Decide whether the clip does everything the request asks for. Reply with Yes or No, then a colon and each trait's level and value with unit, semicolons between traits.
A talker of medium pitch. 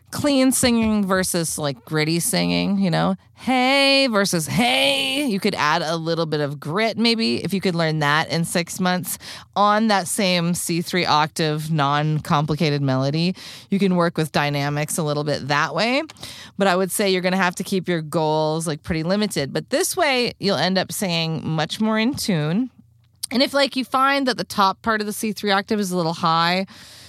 Yes: medium, 180 Hz